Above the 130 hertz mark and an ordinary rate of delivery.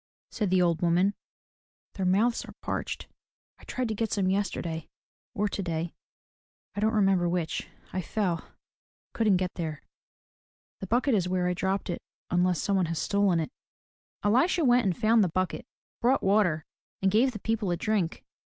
Yes: high, 190 Hz; average, 180 wpm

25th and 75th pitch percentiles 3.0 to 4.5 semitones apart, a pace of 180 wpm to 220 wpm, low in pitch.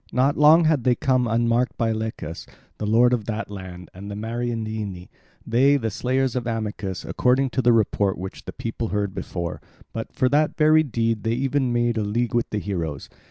Yes: average, 3.4 semitones; average, 190 wpm; low, 115 Hz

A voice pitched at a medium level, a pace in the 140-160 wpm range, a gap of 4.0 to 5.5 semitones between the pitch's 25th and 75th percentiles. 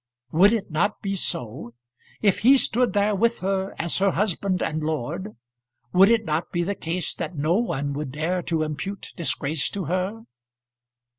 No: medium, 180 Hz; average, 170 wpm; average, 4.4 semitones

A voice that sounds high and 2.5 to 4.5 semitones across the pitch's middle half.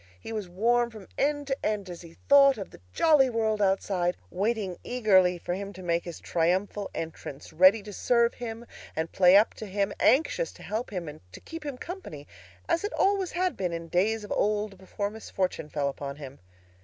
No: high, 205 Hz; average, 5.0 semitones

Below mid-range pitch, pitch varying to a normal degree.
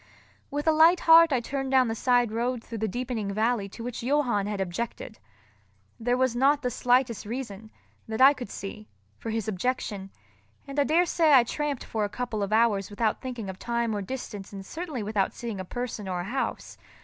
No: high, 235 Hz; average, 3.8 semitones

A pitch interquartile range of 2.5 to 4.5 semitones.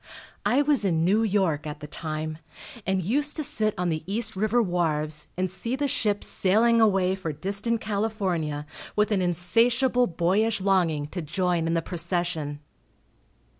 No: average, 4.9 semitones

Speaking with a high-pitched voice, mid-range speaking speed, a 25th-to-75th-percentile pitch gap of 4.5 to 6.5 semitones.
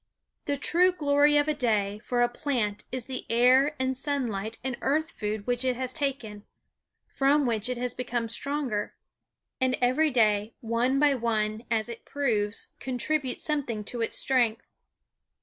No: very high, 250 Hz; average, 160 wpm; average, 3.7 semitones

